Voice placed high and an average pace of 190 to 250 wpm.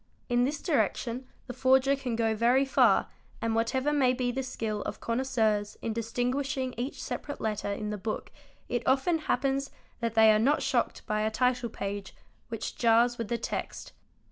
No: high, 245 Hz; average, 175 wpm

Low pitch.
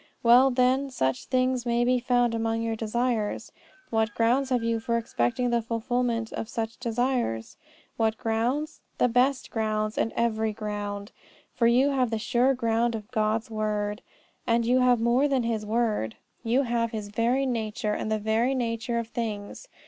No: high, 230 Hz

